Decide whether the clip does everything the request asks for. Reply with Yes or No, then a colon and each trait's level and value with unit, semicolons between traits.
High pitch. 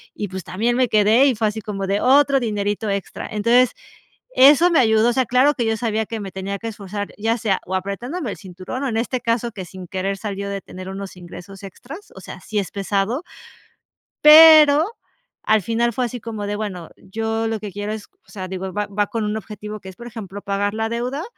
Yes: high, 215 Hz